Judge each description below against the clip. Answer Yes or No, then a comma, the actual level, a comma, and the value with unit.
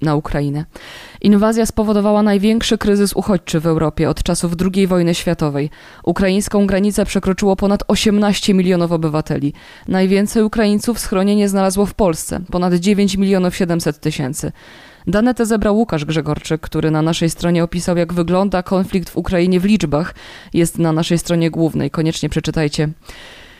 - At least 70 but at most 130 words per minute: No, average, 140 wpm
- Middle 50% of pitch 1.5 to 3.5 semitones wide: No, average, 3.9 semitones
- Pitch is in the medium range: Yes, medium, 180 Hz